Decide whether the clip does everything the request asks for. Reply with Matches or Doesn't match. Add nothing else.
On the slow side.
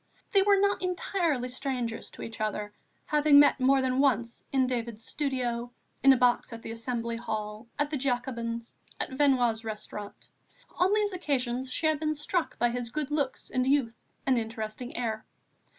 Doesn't match